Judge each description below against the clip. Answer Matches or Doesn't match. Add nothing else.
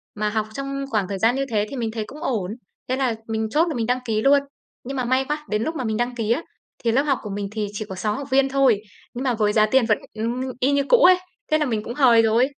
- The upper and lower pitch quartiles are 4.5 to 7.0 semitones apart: Doesn't match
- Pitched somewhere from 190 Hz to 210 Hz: Doesn't match